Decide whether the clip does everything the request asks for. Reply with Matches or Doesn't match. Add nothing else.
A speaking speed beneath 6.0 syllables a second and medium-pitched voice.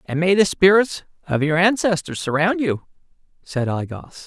Matches